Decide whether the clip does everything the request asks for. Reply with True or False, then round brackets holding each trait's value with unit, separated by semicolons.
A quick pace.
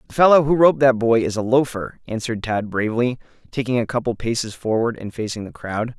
True (220 wpm)